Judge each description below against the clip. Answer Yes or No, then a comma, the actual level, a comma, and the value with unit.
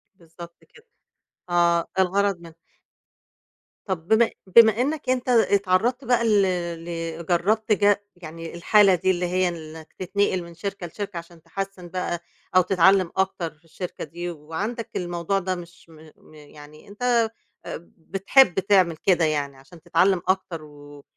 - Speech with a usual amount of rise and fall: Yes, average, 3.2 semitones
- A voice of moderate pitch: Yes, medium, 180 Hz